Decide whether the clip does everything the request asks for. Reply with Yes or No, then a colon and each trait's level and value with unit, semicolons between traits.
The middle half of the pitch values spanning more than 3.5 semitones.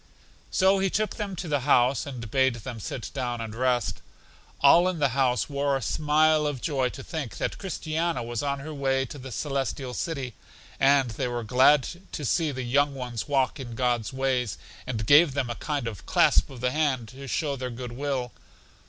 No: average, 3.0 semitones